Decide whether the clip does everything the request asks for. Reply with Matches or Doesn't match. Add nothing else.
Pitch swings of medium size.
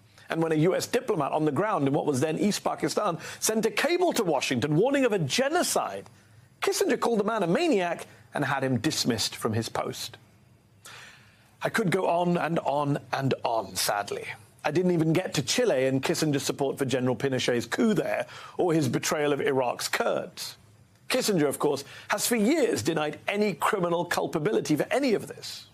Doesn't match